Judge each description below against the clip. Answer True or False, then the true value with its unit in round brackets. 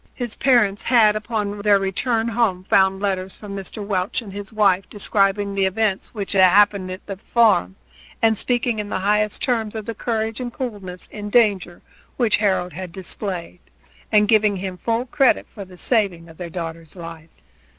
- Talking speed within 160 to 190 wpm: True (175 wpm)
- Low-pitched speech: False (205 Hz)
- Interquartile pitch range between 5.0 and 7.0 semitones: False (2.8 semitones)